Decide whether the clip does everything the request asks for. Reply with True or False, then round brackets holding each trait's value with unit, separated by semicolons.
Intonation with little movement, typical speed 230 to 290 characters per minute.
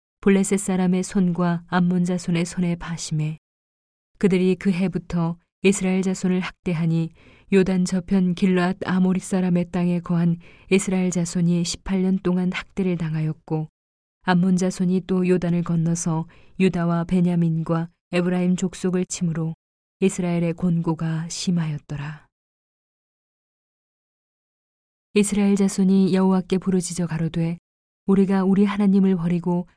True (1.8 semitones; 285 characters per minute)